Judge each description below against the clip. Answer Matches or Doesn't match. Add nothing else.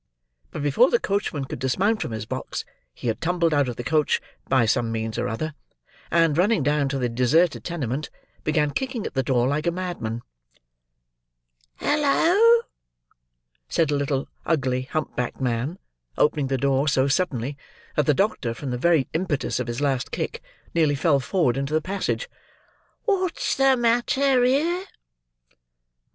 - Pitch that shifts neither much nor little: Doesn't match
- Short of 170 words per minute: Matches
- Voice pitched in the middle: Matches